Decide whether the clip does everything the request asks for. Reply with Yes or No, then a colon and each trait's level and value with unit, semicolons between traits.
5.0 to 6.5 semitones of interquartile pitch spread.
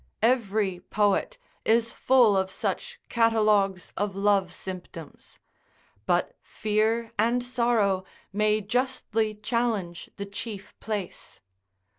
No: average, 2.9 semitones